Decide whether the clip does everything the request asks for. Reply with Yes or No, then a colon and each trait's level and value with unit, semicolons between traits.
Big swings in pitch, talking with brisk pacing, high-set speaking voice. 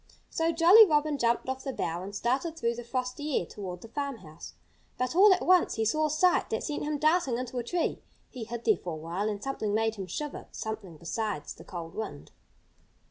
Yes: wide, 6.6 semitones; fast, 215 wpm; high, 240 Hz